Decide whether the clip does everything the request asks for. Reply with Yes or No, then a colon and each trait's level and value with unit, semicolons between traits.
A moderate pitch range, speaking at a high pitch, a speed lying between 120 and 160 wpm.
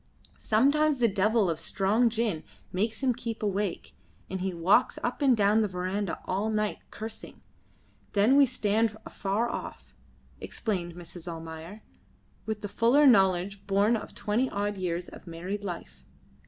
Yes: average, 3.4 semitones; high, 205 Hz; average, 150 wpm